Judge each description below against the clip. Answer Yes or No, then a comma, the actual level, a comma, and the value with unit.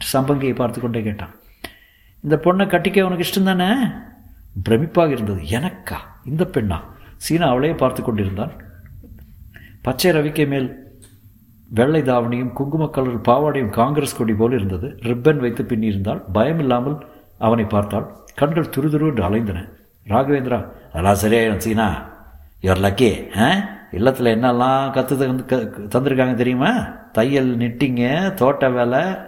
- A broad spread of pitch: No, average, 4.8 semitones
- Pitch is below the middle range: Yes, low, 120 Hz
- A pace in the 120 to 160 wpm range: Yes, average, 125 wpm